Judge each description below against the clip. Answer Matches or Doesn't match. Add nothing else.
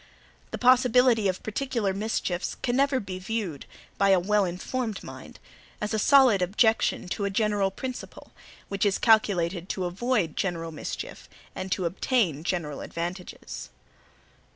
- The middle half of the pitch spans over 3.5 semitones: Matches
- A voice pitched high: Matches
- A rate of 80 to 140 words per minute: Matches